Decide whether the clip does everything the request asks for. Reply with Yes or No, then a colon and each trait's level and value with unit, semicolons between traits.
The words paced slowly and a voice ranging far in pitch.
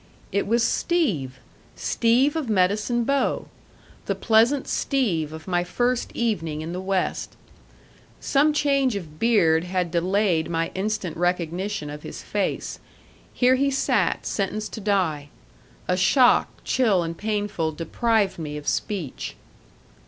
Yes: slow, 130 wpm; wide, 6.0 semitones